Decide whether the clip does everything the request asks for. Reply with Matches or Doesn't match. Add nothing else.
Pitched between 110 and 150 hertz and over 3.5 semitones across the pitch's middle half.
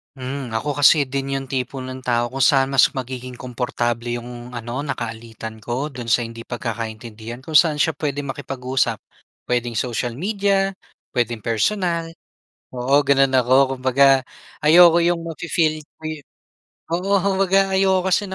Matches